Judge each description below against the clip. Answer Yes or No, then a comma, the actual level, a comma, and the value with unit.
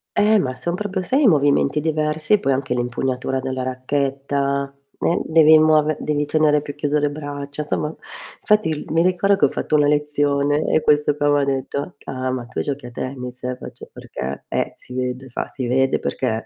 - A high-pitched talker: No, medium, 145 Hz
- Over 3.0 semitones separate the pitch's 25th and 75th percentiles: No, average, 2.7 semitones